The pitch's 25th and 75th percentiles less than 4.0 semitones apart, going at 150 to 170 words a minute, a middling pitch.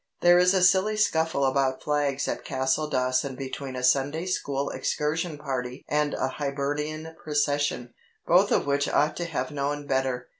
Yes: average, 2.8 semitones; average, 155 wpm; medium, 145 Hz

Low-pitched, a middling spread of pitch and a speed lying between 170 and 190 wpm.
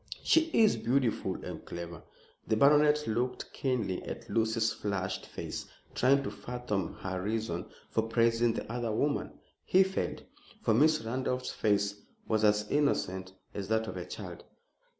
No: low, 115 Hz; average, 4.1 semitones; average, 150 wpm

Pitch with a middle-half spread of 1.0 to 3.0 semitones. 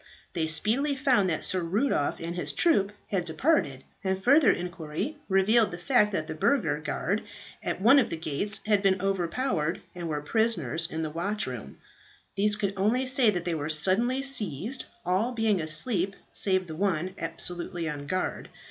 No: average, 5.1 semitones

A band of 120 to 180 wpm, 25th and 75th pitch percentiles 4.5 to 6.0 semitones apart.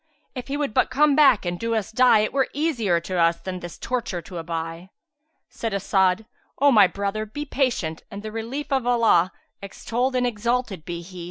No: average, 195 wpm; wide, 5.6 semitones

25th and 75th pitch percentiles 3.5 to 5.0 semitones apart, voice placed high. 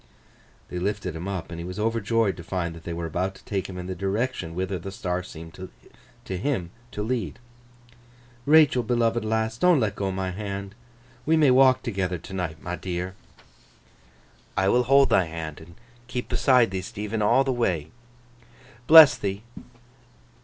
No: average, 4.5 semitones; very low, 95 Hz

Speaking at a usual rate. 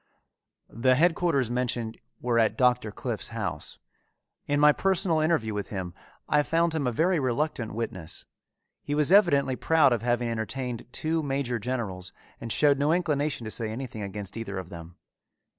Yes: average, 160 wpm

